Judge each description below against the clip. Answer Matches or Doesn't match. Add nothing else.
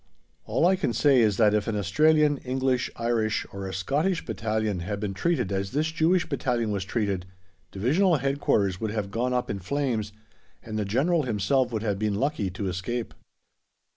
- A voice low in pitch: Matches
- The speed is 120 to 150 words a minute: Doesn't match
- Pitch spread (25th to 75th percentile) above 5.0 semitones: Matches